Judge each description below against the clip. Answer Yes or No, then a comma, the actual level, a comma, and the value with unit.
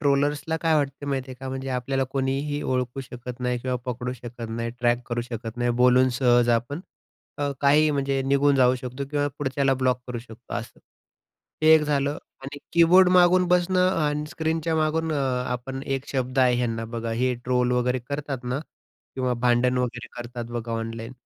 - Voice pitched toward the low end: Yes, low, 130 Hz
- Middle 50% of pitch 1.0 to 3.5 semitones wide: Yes, average, 2.8 semitones